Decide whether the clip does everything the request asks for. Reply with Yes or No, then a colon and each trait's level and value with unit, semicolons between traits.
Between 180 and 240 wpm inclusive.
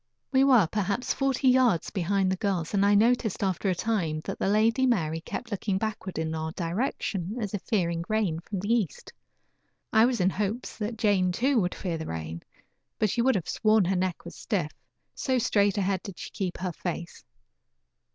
Yes: average, 195 wpm